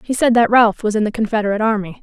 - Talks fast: Yes, fast, 265 wpm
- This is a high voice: Yes, high, 220 Hz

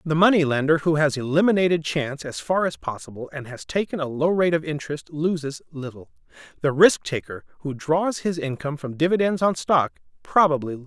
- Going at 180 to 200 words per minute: Yes, average, 195 wpm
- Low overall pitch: No, medium, 155 Hz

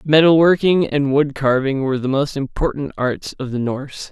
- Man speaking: Yes, male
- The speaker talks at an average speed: Yes, average, 190 wpm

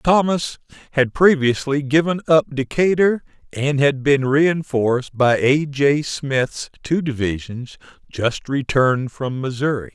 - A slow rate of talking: Yes, slow, 120 wpm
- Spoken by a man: Yes, male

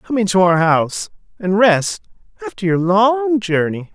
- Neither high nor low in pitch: Yes, medium, 175 Hz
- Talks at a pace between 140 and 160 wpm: Yes, average, 150 wpm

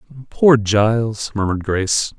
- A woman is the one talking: No, male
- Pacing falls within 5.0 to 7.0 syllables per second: Yes, 5.2 syllables/s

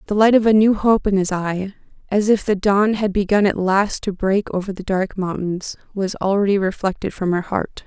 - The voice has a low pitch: No, high, 195 Hz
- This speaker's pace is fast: Yes, fast, 220 wpm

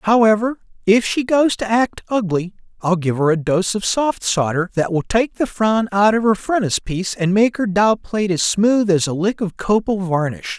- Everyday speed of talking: No, fast, 210 wpm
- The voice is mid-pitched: No, high, 205 Hz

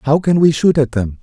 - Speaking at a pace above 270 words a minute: Yes, fast, 295 wpm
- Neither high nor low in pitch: Yes, medium, 145 Hz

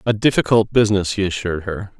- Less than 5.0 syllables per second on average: No, 6.6 syllables/s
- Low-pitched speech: Yes, low, 100 Hz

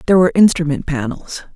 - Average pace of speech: Yes, average, 155 wpm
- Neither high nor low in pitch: Yes, medium, 165 Hz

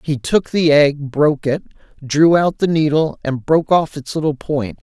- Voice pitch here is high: No, medium, 150 Hz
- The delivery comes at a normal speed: Yes, average, 195 wpm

